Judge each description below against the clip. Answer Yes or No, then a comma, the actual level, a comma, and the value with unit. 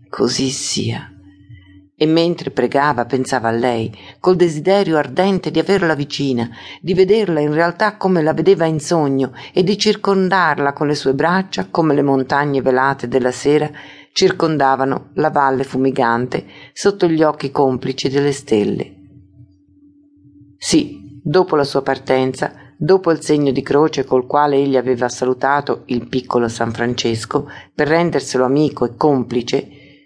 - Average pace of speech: Yes, average, 140 wpm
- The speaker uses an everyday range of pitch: Yes, average, 3.8 semitones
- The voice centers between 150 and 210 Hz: No, medium, 140 Hz